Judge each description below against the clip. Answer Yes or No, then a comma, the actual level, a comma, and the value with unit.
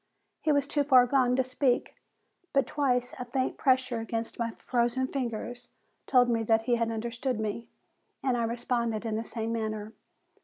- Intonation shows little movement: Yes, narrow, 2.2 semitones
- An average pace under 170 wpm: No, average, 175 wpm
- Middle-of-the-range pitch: No, high, 240 Hz